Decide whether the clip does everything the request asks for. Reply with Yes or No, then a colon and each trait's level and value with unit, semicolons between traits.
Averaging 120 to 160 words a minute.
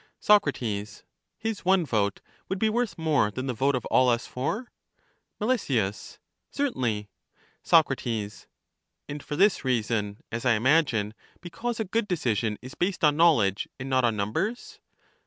Yes: average, 150 wpm